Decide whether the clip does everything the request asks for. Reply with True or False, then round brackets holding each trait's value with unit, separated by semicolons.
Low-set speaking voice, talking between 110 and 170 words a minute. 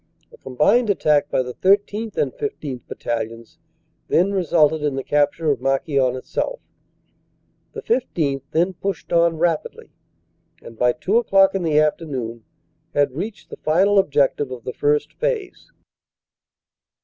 False (155 Hz; 150 wpm)